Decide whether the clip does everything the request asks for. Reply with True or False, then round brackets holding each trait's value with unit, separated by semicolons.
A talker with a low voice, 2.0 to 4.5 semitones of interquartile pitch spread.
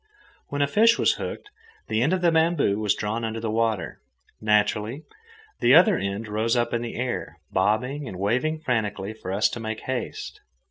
False (115 Hz; 5.0 semitones)